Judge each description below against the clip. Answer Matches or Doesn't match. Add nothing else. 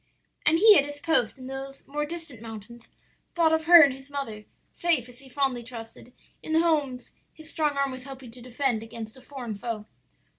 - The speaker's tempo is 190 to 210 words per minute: Matches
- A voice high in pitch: Matches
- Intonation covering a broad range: Doesn't match